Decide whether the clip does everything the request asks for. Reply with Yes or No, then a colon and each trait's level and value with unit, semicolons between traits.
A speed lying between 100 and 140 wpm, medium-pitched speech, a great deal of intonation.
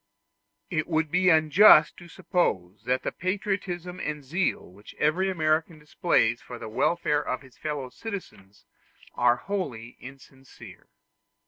Yes: slow, 135 wpm; medium, 155 Hz; wide, 5.9 semitones